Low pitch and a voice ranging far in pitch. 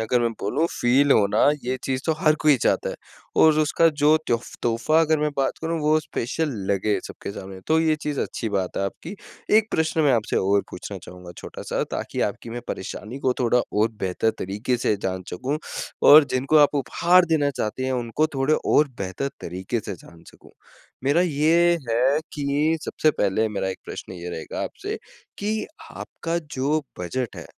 Yes: low, 130 Hz; wide, 6.6 semitones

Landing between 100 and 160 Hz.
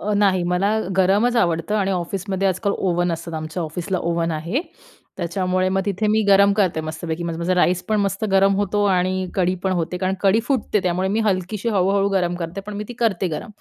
No: medium, 185 Hz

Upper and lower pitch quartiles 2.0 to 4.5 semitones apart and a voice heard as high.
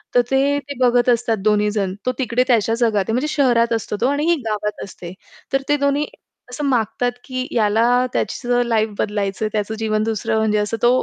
Yes: average, 3.0 semitones; high, 230 Hz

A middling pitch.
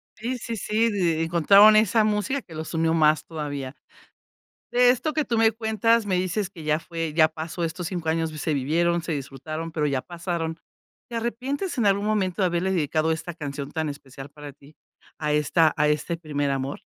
Yes: medium, 165 Hz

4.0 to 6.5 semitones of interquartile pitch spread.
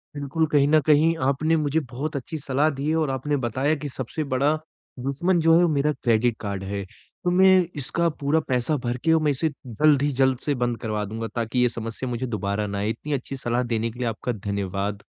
Yes: average, 4.6 semitones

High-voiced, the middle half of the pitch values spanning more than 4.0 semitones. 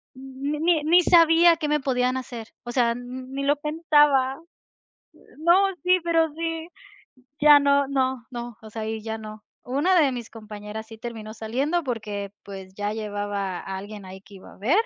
Yes: very high, 255 Hz; wide, 5.6 semitones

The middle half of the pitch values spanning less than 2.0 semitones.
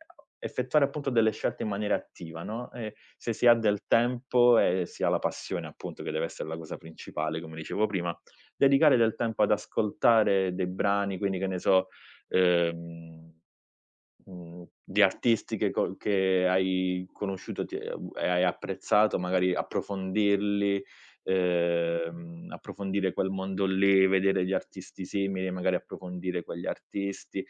No: average, 2.7 semitones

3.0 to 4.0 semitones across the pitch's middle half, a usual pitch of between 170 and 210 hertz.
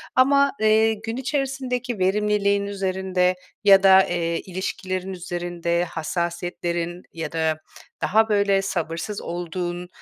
Yes: average, 3.3 semitones; high, 190 Hz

